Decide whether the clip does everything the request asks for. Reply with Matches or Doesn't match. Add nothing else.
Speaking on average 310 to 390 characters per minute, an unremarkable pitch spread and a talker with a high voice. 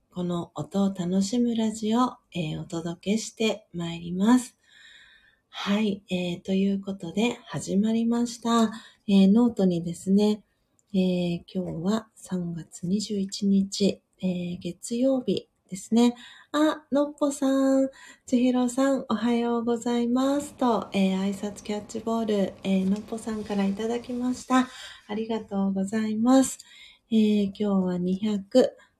Doesn't match